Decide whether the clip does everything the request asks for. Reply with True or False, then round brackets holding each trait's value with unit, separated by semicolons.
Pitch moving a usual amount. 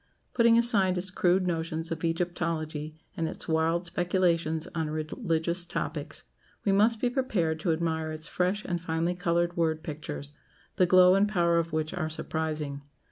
False (2.3 semitones)